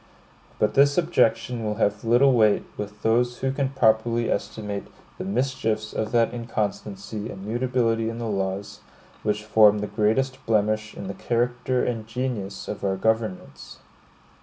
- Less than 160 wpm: Yes, average, 150 wpm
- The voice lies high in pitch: No, low, 110 Hz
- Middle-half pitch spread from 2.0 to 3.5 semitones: Yes, average, 2.7 semitones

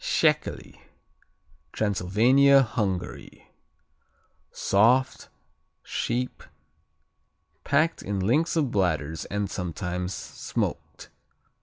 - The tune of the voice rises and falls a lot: Yes, wide, 6.2 semitones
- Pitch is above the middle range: No, low, 105 Hz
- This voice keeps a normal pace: No, slow, 65 wpm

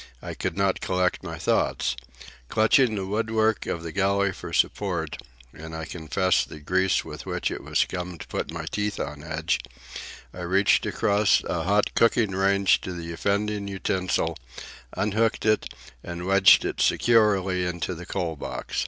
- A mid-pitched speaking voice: No, very low, 95 Hz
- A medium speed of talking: Yes, average, 155 wpm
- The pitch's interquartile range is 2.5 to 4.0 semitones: Yes, average, 3.3 semitones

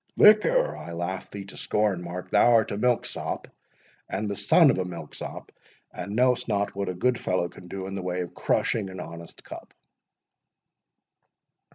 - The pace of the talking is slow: No, average, 165 wpm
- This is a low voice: Yes, very low, 95 Hz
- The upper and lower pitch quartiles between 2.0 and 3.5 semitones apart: Yes, average, 3.2 semitones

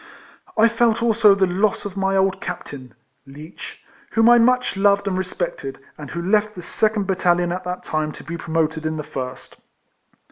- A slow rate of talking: No, average, 180 wpm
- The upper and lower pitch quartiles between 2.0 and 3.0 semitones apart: No, average, 4.7 semitones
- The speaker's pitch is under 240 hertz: Yes, high, 190 Hz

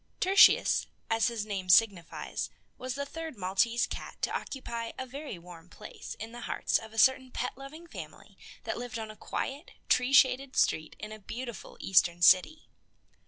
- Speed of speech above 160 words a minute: Yes, average, 170 wpm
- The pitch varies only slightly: No, average, 4.6 semitones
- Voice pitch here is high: Yes, high, 235 Hz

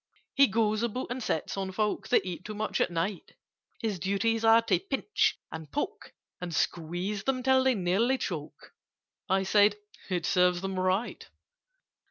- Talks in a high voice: Yes, high, 205 Hz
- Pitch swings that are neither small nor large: Yes, average, 4.2 semitones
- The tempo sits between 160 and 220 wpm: Yes, average, 165 wpm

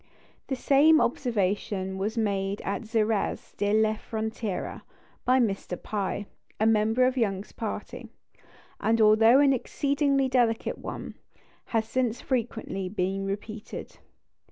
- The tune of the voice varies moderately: Yes, average, 3.5 semitones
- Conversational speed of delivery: No, slow, 120 wpm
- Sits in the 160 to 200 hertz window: No, high, 220 Hz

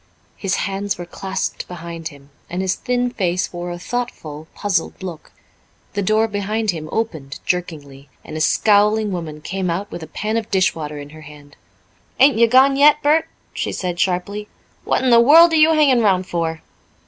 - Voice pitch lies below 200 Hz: Yes, high, 190 Hz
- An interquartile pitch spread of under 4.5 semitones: No, average, 5.3 semitones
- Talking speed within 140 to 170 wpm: No, average, 185 wpm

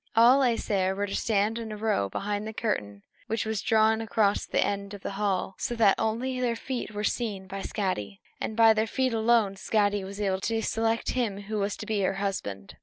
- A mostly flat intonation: Yes, narrow, 2.3 semitones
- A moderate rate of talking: No, fast, 215 wpm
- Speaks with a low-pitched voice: No, high, 210 Hz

